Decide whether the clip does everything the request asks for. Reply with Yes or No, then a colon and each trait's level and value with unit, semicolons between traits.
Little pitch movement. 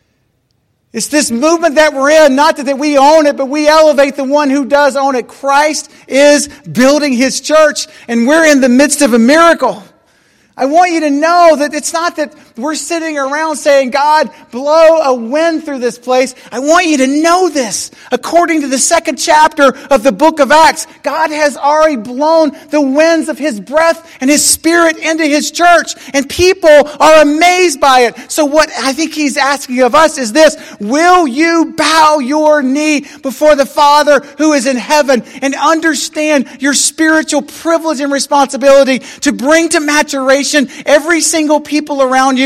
Yes: narrow, 2.3 semitones